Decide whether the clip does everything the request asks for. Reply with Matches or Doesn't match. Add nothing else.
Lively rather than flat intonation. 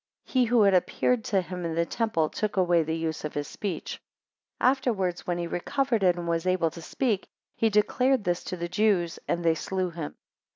Doesn't match